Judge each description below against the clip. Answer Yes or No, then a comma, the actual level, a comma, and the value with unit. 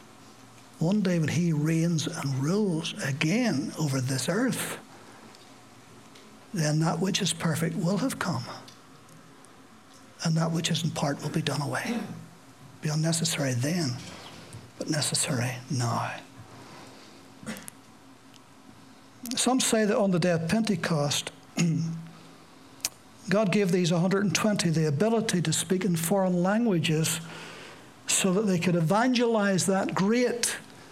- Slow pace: Yes, slow, 120 wpm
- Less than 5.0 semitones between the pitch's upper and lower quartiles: Yes, average, 4.3 semitones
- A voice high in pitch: No, medium, 170 Hz